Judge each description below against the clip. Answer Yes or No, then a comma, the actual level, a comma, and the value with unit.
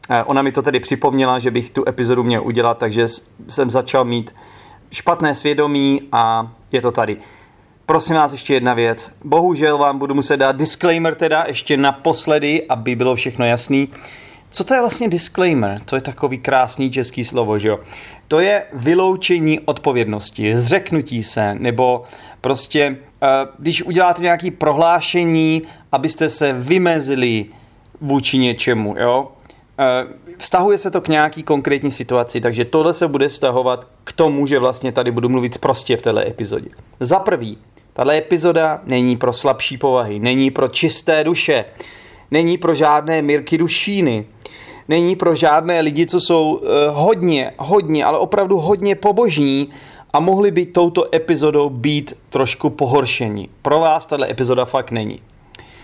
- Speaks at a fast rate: No, average, 145 wpm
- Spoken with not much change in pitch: No, average, 4.6 semitones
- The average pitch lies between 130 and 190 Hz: Yes, medium, 140 Hz